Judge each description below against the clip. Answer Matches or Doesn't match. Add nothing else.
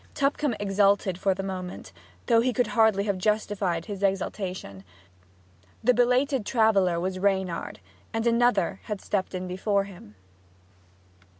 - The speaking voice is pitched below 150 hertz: Doesn't match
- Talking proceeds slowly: Matches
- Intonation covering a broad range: Doesn't match